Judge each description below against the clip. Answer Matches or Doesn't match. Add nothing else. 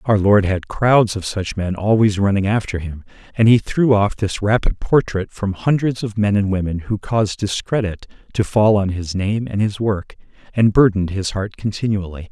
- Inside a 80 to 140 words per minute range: Doesn't match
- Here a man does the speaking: Matches